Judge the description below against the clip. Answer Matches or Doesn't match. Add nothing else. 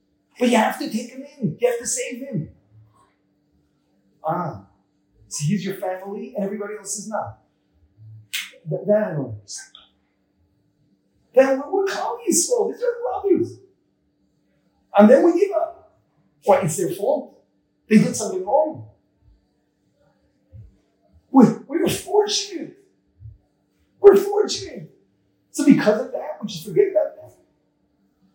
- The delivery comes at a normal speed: Doesn't match